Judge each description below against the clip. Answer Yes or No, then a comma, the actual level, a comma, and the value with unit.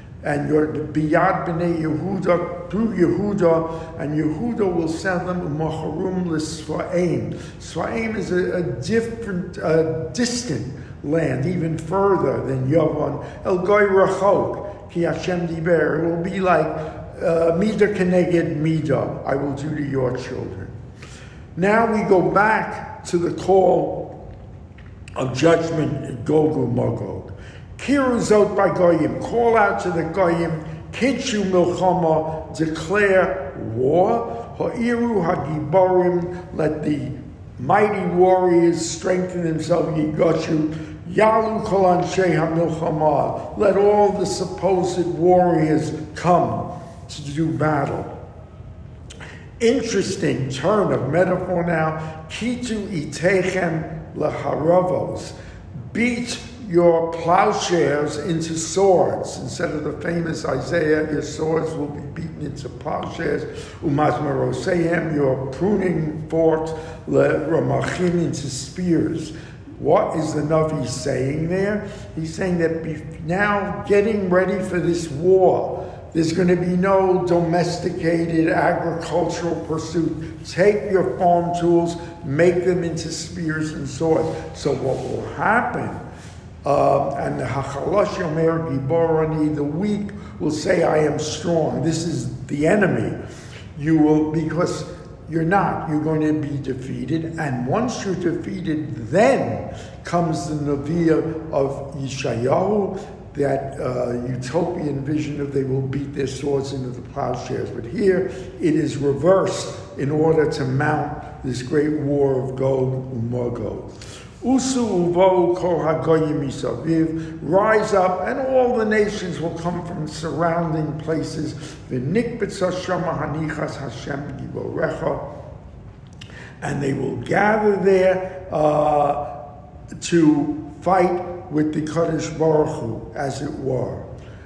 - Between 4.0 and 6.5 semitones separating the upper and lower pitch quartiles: No, average, 3.3 semitones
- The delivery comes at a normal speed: No, slow, 110 wpm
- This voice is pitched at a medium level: Yes, medium, 165 Hz